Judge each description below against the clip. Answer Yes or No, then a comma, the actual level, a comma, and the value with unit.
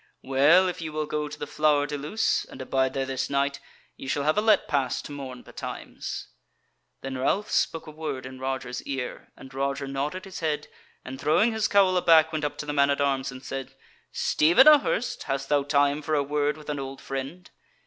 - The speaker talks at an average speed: No, fast, 215 wpm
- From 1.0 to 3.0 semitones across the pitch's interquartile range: Yes, narrow, 2.6 semitones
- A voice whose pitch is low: No, medium, 145 Hz